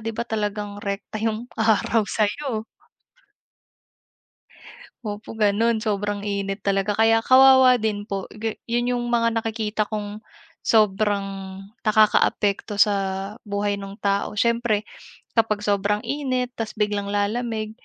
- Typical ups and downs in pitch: No, narrow, 1.9 semitones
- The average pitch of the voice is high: Yes, high, 215 Hz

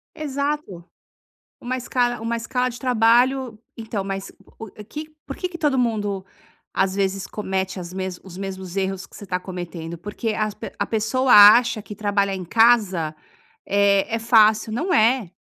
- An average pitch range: Yes, average, 3.9 semitones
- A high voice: Yes, high, 215 Hz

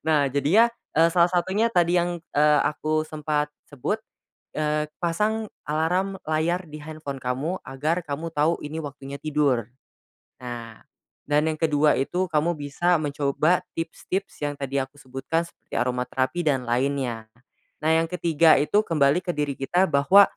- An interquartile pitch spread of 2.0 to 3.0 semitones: No, average, 3.4 semitones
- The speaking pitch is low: No, medium, 150 Hz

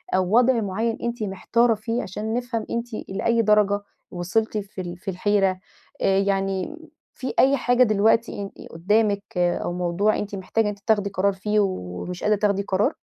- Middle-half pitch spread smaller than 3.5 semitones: Yes, average, 2.8 semitones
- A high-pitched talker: Yes, high, 205 Hz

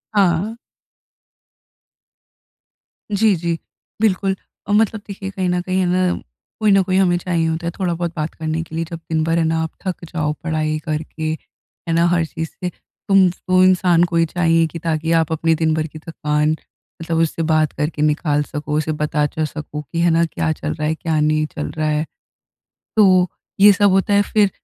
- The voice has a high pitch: No, medium, 165 Hz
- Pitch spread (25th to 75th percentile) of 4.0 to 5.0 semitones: No, average, 2.8 semitones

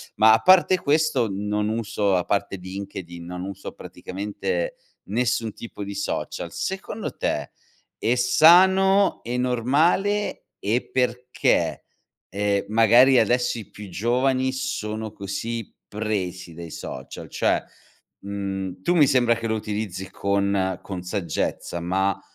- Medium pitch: No, low, 110 Hz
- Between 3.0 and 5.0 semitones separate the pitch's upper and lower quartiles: Yes, average, 4.3 semitones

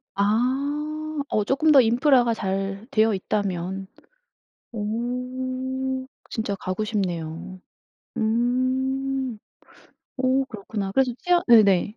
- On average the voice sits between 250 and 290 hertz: No, high, 235 Hz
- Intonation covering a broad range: No, average, 4.5 semitones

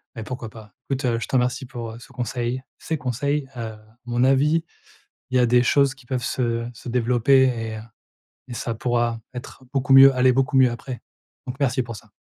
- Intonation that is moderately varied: No, narrow, 2.1 semitones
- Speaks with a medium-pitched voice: No, low, 125 Hz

